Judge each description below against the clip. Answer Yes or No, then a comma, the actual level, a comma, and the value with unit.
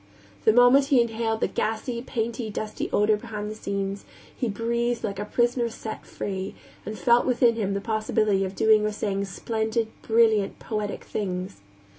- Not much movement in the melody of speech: Yes, narrow, 2.3 semitones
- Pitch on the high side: Yes, high, 220 Hz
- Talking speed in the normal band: Yes, average, 165 wpm